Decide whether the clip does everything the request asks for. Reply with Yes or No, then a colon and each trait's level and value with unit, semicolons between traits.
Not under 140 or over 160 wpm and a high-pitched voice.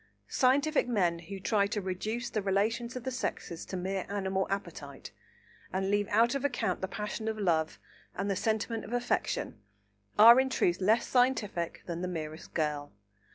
No: average, 170 wpm; high, 200 Hz